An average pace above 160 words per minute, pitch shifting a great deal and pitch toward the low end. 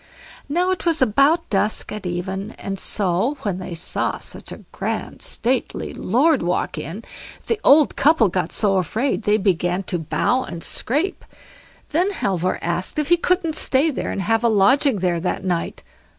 No: average, 170 wpm; wide, 8.0 semitones; high, 215 Hz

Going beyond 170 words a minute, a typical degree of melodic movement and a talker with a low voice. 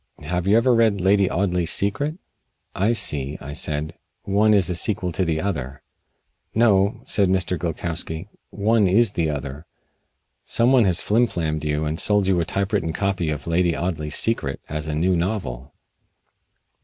No: average, 165 wpm; average, 4.5 semitones; very low, 90 Hz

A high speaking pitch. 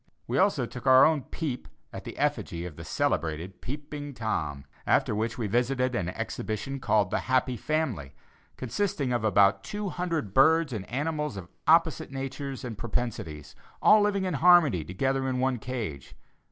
No: low, 130 Hz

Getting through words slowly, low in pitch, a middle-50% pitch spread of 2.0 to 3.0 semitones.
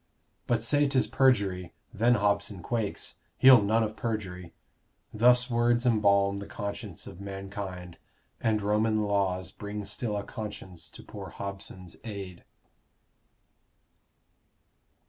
Yes: slow, 115 wpm; low, 105 Hz; narrow, 2.6 semitones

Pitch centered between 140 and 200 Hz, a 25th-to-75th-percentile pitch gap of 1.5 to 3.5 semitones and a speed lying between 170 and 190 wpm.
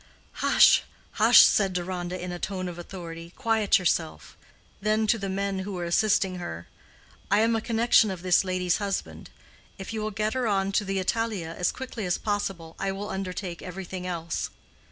Yes: high, 190 Hz; average, 3.0 semitones; average, 180 wpm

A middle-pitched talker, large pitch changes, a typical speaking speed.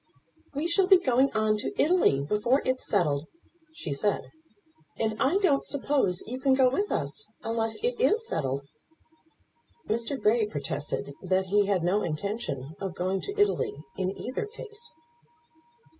No: high, 225 Hz; wide, 7.6 semitones; average, 150 wpm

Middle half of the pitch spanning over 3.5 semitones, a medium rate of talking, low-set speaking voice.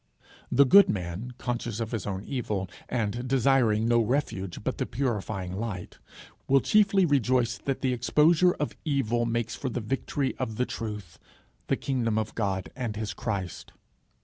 Yes: average, 4.1 semitones; average, 160 wpm; low, 120 Hz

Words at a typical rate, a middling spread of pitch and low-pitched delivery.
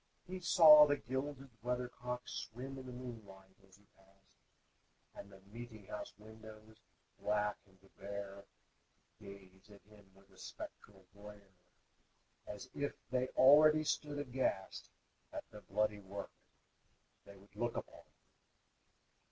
No: slow, 125 wpm; average, 4.4 semitones; low, 110 Hz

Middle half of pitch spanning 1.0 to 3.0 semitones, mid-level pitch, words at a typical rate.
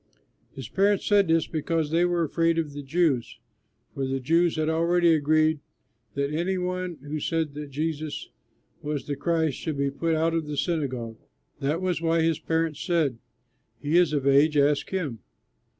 Yes: narrow, 2.6 semitones; medium, 160 Hz; average, 175 wpm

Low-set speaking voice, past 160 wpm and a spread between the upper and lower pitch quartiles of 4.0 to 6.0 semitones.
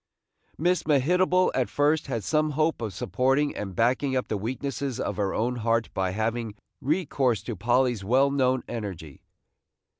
No: low, 125 Hz; average, 155 wpm; average, 4.5 semitones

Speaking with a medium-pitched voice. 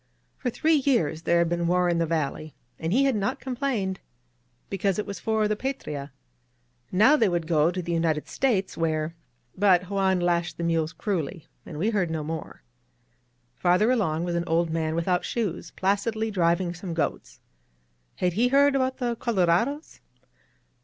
Yes: medium, 180 Hz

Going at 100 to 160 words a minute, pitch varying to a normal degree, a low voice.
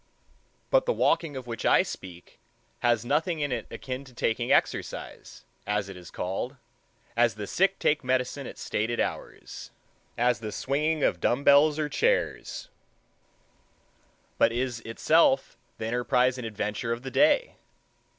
Yes: average, 145 wpm; average, 4.0 semitones; low, 125 Hz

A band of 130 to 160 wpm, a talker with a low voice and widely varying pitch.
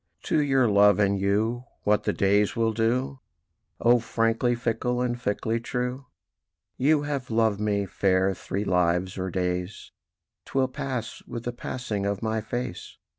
No: average, 150 wpm; low, 115 Hz; average, 3.6 semitones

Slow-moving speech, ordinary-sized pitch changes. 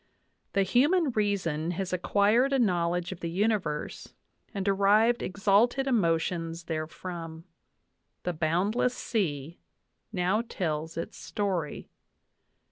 Yes: slow, 105 wpm; average, 4.4 semitones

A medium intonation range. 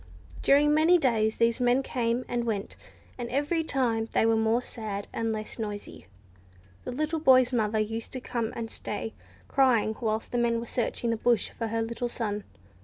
No: narrow, 2.3 semitones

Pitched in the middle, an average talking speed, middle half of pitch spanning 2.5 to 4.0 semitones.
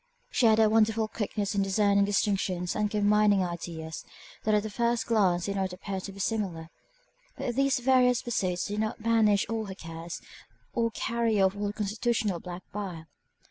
No: high, 205 Hz; average, 180 wpm; average, 2.8 semitones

